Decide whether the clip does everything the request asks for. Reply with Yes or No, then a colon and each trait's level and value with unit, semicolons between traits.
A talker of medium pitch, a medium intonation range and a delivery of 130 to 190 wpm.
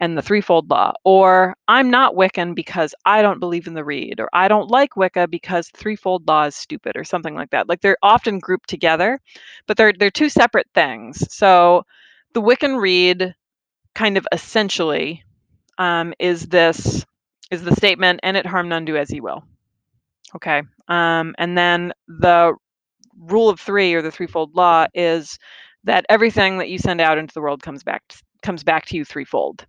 Yes: medium, 180 Hz; average, 3.1 semitones; average, 185 wpm